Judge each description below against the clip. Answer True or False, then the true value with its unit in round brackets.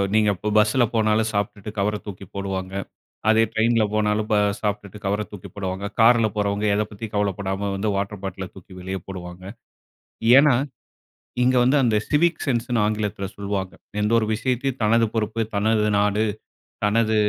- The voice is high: False (105 Hz)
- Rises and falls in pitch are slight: True (2.1 semitones)